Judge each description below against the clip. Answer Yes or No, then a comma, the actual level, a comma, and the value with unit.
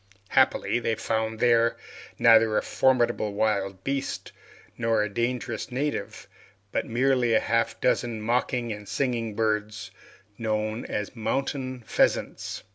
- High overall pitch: No, low, 115 Hz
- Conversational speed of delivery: No, slow, 120 wpm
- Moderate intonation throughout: No, narrow, 2.2 semitones